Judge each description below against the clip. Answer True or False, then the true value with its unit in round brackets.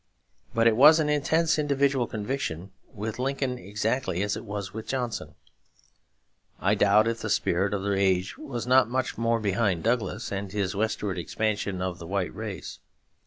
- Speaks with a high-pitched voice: False (110 Hz)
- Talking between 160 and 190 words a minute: True (165 wpm)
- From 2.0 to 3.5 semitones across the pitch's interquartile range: False (4.3 semitones)